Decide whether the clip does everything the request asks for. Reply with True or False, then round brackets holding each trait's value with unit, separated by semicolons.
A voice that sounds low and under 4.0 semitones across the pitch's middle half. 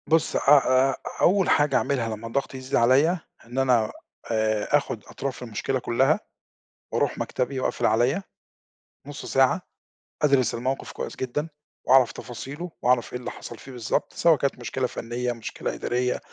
True (130 Hz; 2.5 semitones)